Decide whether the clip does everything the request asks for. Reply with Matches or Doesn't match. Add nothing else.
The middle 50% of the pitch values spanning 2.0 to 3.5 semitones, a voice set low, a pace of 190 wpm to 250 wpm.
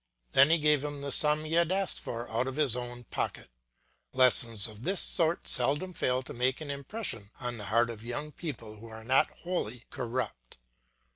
Doesn't match